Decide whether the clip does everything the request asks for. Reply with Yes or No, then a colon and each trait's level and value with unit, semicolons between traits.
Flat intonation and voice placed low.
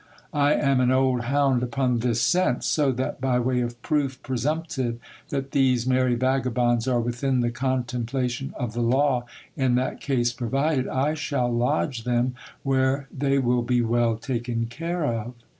Yes: narrow, 2.1 semitones; low, 125 Hz